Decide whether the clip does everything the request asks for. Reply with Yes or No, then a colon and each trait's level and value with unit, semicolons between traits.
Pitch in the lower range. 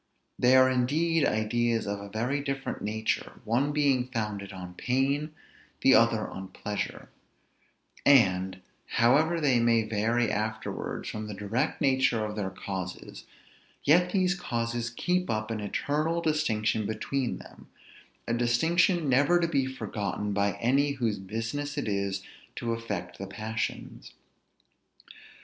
Yes: low, 120 Hz